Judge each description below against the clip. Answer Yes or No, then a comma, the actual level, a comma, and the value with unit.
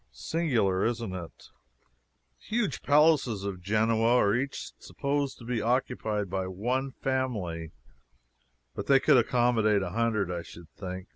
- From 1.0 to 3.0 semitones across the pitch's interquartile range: No, wide, 5.6 semitones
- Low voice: Yes, low, 110 Hz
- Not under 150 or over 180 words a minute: No, average, 140 wpm